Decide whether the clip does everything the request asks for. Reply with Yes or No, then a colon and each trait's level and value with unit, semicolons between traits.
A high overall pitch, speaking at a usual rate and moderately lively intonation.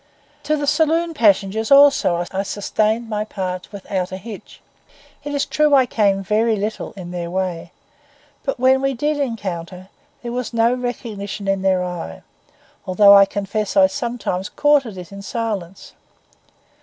Yes: high, 210 Hz; average, 150 wpm; average, 4.5 semitones